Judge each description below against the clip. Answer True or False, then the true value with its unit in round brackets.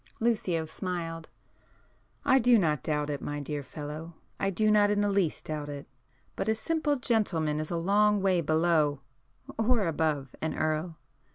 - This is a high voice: False (165 Hz)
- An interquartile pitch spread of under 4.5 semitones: False (5.5 semitones)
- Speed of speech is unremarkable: True (150 wpm)